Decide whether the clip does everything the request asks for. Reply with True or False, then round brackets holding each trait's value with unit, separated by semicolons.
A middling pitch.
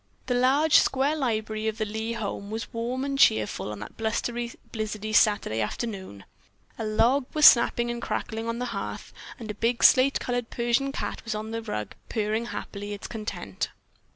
False (225 Hz)